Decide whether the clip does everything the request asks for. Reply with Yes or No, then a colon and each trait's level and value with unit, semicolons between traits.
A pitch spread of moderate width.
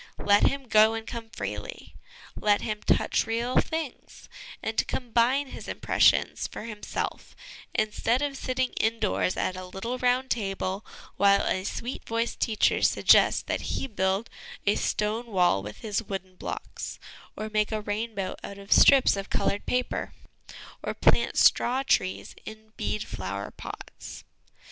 Yes: average, 3.2 semitones